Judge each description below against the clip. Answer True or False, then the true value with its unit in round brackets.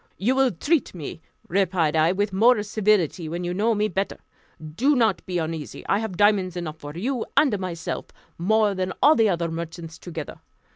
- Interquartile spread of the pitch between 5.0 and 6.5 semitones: False (4.2 semitones)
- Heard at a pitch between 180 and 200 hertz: True (190 Hz)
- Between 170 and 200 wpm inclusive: True (185 wpm)